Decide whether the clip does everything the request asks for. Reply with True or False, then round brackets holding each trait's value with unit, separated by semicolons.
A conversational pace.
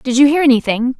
False (240 wpm)